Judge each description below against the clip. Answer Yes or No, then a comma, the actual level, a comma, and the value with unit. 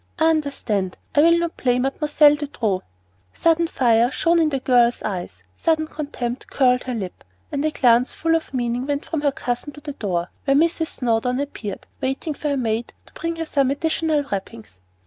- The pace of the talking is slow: No, average, 190 wpm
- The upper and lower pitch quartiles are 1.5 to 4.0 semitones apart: No, average, 4.5 semitones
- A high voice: Yes, very high, 275 Hz